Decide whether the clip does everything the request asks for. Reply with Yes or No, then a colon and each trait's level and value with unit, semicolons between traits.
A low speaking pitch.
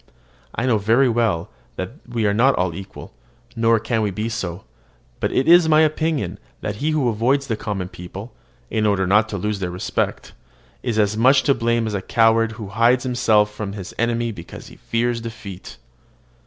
Yes: low, 110 Hz